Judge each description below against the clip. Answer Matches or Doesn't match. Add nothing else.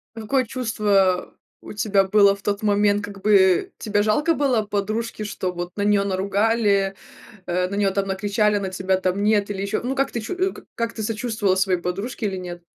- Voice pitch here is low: Doesn't match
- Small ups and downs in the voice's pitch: Matches